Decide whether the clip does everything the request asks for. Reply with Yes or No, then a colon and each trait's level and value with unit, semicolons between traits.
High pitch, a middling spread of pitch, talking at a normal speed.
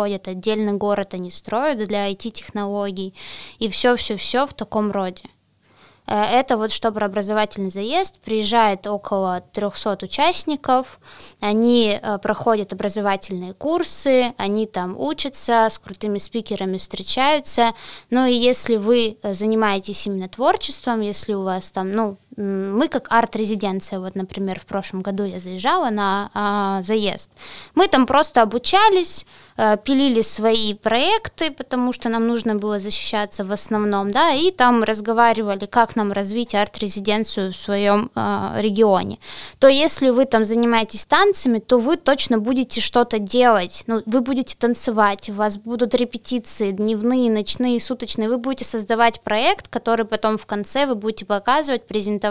Yes: high, 220 Hz; average, 3.2 semitones; average, 140 wpm